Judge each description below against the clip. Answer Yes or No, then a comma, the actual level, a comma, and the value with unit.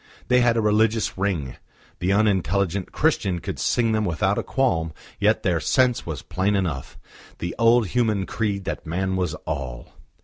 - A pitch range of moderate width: Yes, average, 4.3 semitones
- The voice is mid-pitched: No, low, 100 Hz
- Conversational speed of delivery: Yes, average, 165 wpm